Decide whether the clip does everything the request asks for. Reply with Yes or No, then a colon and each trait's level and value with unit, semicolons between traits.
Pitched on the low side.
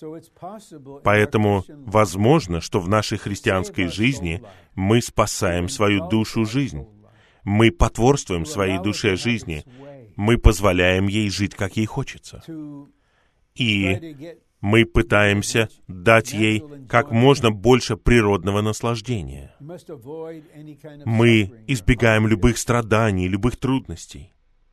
Yes: low, 110 Hz